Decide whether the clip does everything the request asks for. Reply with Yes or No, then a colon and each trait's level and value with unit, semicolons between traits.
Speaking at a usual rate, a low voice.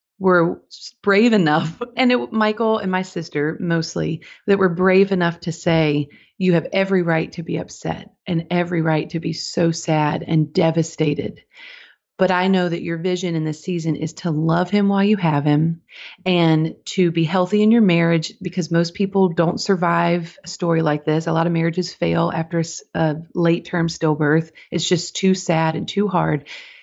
No: average, 185 wpm; medium, 170 Hz